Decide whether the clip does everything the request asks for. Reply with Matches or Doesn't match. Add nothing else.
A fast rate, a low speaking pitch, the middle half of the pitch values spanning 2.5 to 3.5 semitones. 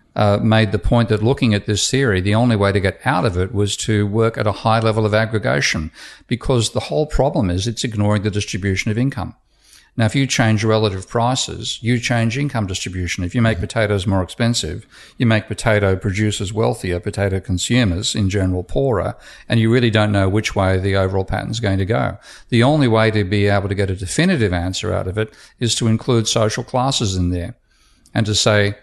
Matches